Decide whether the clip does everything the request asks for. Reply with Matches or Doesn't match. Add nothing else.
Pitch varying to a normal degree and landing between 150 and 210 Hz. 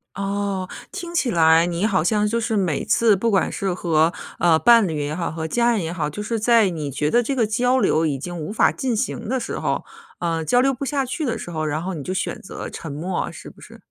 Doesn't match